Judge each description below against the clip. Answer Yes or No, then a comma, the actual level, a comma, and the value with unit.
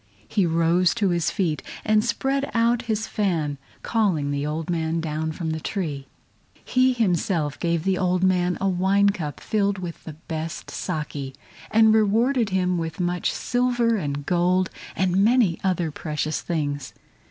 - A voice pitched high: No, medium, 180 Hz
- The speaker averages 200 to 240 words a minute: No, average, 155 wpm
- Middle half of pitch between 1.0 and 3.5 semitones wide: No, average, 4.8 semitones